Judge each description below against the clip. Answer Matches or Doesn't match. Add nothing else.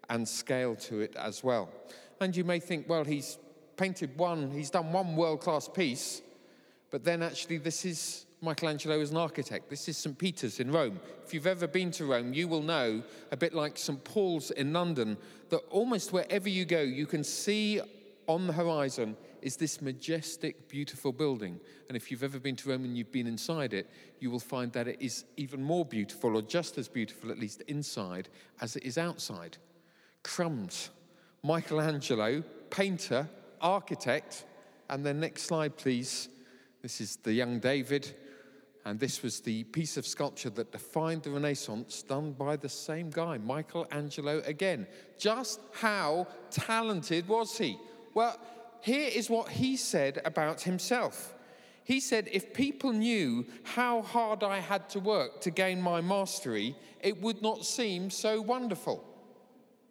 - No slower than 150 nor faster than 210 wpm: Matches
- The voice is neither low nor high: Matches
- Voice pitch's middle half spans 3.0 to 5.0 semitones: Doesn't match